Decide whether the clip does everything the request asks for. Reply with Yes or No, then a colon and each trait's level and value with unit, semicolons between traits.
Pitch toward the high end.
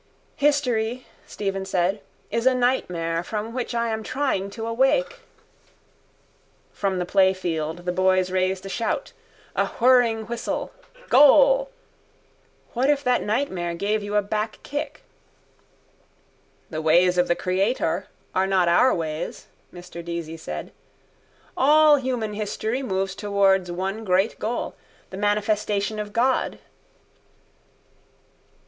Yes: high, 205 Hz